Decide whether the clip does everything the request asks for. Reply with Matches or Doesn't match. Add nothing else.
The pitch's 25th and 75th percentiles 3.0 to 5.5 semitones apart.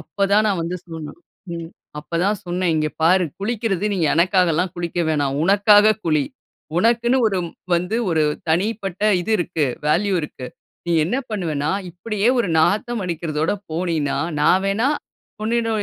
Matches